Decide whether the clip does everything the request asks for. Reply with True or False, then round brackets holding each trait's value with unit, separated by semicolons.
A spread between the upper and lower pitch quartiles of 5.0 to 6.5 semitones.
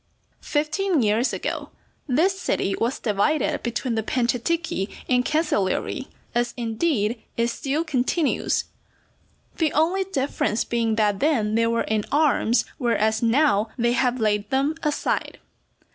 True (5.4 semitones)